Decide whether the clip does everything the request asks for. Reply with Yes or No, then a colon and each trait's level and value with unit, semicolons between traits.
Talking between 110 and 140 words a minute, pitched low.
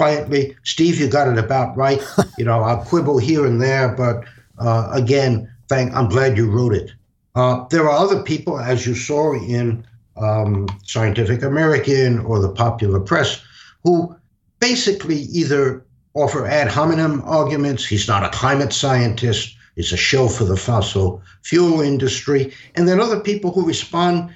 No: average, 160 wpm; low, 130 Hz